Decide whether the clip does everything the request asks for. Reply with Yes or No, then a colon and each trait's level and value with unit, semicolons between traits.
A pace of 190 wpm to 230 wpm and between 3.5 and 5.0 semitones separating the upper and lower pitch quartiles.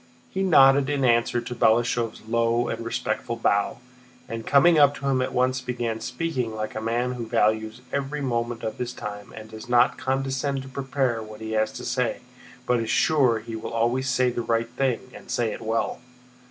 No: average, 195 wpm; average, 2.7 semitones